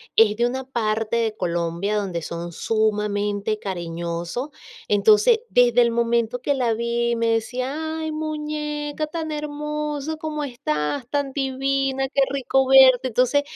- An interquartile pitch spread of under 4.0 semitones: No, average, 5.1 semitones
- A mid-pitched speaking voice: No, high, 245 Hz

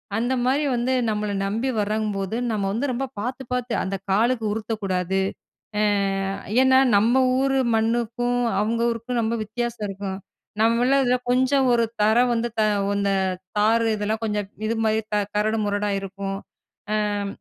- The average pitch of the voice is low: No, high, 225 Hz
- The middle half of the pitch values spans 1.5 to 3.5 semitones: Yes, average, 2.8 semitones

